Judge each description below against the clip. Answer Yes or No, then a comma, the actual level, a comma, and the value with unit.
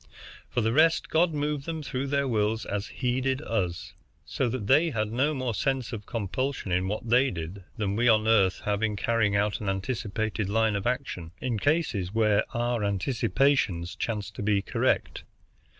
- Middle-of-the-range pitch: No, low, 115 Hz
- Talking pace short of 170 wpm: No, average, 180 wpm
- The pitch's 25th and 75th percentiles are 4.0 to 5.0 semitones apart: Yes, average, 4.4 semitones